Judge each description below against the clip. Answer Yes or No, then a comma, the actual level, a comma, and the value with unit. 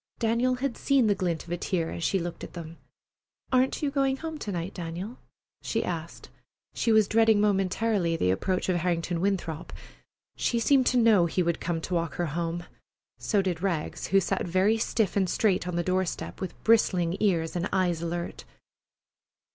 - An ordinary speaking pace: Yes, average, 190 wpm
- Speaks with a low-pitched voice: No, medium, 185 Hz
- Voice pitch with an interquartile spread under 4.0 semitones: No, average, 4.5 semitones